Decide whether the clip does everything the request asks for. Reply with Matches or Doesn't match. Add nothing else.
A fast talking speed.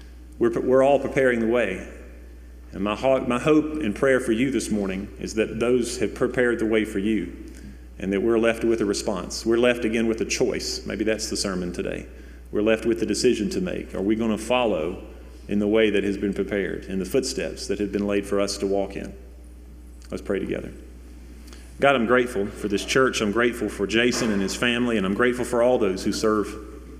Matches